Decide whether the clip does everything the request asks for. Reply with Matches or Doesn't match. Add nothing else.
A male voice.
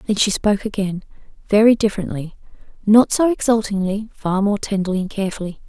Doesn't match